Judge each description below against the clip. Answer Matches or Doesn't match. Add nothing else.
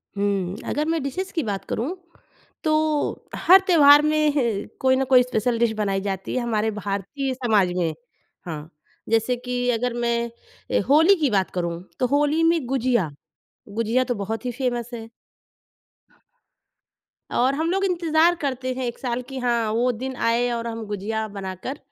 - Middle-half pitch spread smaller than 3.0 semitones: Doesn't match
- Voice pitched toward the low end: Doesn't match